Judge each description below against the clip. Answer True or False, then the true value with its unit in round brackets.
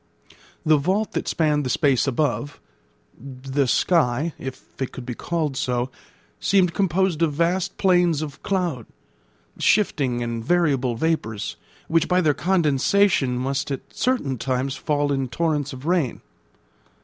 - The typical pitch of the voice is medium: True (145 Hz)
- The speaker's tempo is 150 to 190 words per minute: False (135 wpm)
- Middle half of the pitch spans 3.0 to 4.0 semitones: False (4.6 semitones)